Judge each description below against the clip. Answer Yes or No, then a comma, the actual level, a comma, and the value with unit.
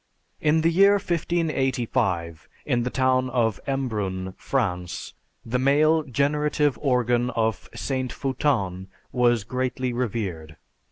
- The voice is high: No, low, 125 Hz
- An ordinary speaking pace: No, slow, 110 wpm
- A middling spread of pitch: Yes, average, 4.0 semitones